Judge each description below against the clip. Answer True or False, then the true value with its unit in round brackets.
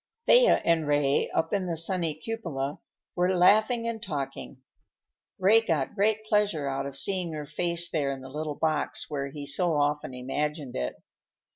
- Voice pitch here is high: False (160 Hz)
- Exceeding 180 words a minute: False (165 wpm)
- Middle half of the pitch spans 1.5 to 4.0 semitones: False (4.8 semitones)